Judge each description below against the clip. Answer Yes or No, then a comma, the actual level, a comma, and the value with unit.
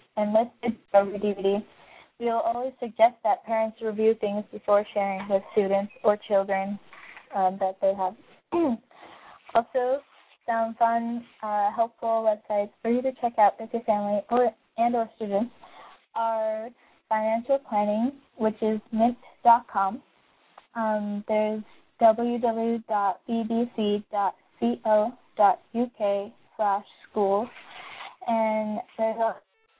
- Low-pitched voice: No, high, 220 Hz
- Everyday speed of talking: No, slow, 115 wpm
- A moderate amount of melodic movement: No, narrow, 2.1 semitones